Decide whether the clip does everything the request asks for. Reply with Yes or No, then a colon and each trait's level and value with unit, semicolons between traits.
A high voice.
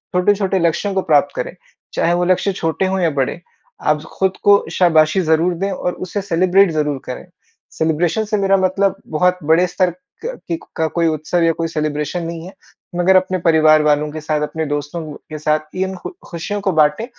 No: medium, 170 Hz